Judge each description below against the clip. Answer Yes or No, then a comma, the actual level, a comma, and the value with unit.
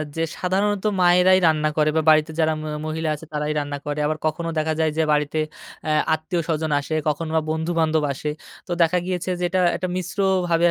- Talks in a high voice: No, medium, 160 Hz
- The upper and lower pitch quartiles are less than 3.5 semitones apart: Yes, narrow, 2.4 semitones